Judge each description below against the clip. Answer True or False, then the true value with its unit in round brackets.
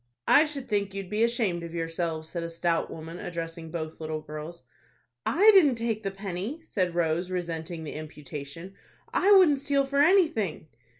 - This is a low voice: False (175 Hz)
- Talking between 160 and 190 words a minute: True (170 wpm)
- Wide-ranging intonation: True (6.3 semitones)